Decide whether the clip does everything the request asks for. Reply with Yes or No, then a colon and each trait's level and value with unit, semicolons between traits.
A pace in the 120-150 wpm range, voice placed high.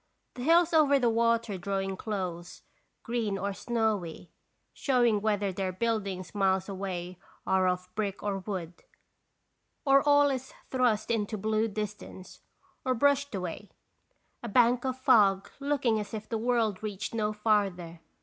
Yes: average, 145 wpm; high, 210 Hz